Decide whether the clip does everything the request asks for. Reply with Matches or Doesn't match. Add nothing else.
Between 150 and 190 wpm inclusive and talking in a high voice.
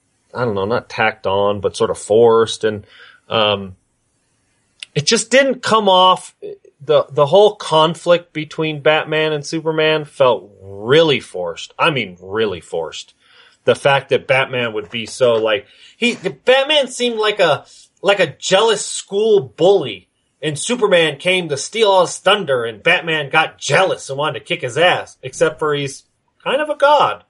Matches